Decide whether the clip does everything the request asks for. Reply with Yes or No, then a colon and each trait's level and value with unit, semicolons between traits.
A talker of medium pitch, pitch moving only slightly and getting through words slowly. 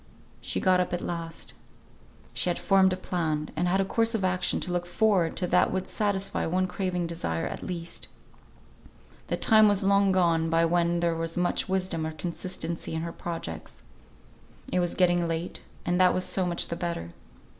No: medium, 175 Hz; narrow, 2.0 semitones; average, 190 wpm